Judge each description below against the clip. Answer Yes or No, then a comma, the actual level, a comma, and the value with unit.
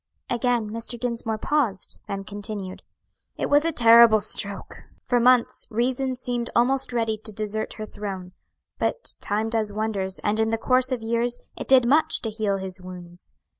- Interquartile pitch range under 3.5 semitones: Yes, average, 2.9 semitones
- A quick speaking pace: No, average, 170 wpm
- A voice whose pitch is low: No, high, 225 Hz